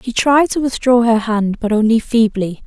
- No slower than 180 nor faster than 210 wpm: Yes, average, 200 wpm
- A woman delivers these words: Yes, female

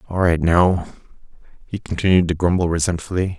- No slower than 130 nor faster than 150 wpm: Yes, average, 140 wpm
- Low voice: Yes, very low, 90 Hz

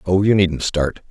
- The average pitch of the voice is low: Yes, very low, 90 Hz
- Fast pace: Yes, fast, 220 wpm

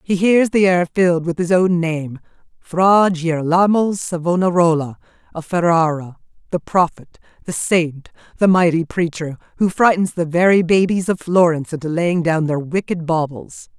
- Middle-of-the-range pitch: Yes, medium, 170 Hz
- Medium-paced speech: Yes, average, 145 wpm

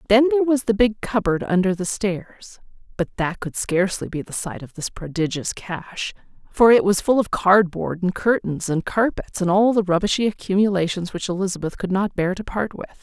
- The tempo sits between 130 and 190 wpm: No, average, 200 wpm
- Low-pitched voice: No, high, 195 Hz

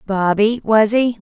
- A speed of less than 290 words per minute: Yes, average, 140 wpm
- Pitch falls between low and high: No, high, 215 Hz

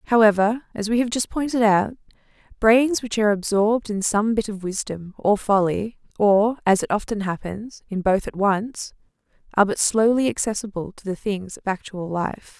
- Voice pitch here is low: No, high, 210 Hz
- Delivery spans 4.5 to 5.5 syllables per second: Yes, 5.0 syllables/s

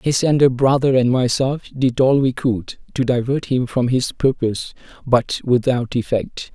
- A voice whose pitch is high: No, low, 125 Hz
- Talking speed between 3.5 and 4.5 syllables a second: Yes, 4.4 syllables/s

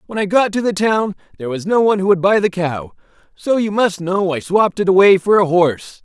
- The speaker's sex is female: No, male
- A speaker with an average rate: No, fast, 260 wpm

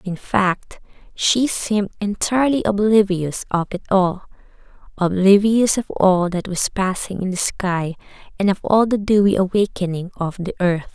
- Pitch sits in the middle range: No, high, 195 Hz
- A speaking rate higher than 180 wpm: No, average, 140 wpm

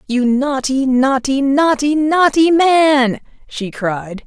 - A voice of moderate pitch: No, very high, 275 Hz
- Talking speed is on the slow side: Yes, slow, 115 wpm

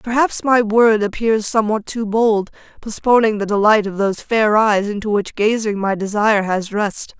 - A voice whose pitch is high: Yes, high, 215 Hz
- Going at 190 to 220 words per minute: No, average, 175 wpm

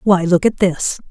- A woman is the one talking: Yes, female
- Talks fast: Yes, fast, 215 wpm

